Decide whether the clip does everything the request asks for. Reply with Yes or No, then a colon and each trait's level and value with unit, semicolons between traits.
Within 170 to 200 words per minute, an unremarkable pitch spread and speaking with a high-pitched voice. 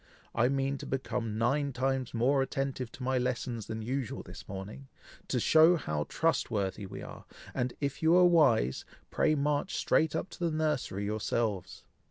No: average, 175 wpm; average, 4.2 semitones; low, 130 Hz